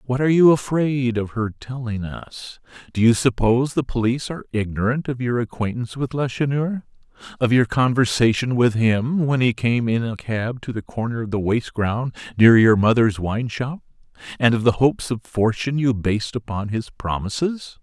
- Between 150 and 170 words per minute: No, average, 180 wpm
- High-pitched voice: No, low, 120 Hz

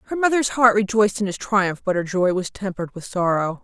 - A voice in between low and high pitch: No, high, 200 Hz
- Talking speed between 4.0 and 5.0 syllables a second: No, 5.9 syllables/s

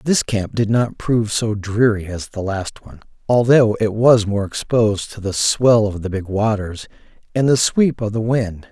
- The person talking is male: Yes, male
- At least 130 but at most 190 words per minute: No, average, 200 wpm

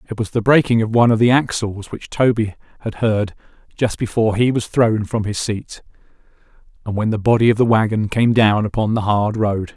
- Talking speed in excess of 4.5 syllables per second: Yes, 5.5 syllables/s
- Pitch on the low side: Yes, low, 110 Hz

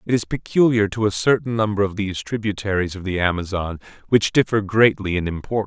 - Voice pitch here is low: Yes, low, 100 Hz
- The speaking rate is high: No, average, 190 wpm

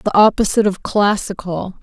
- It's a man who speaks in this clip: No, female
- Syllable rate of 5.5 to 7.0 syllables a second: Yes, 5.6 syllables/s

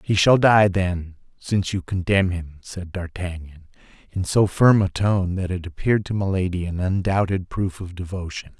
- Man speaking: Yes, male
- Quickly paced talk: No, average, 175 wpm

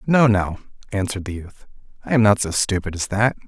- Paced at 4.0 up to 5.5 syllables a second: No, 5.8 syllables/s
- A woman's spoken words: No, male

